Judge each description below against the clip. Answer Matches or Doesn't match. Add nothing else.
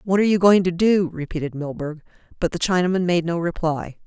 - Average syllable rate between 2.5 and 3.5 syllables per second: Doesn't match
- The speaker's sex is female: Matches